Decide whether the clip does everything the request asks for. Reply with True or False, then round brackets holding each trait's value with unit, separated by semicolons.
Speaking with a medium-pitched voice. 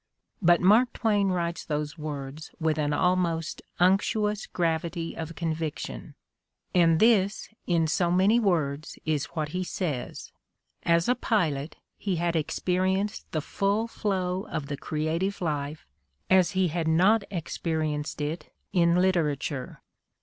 True (170 Hz)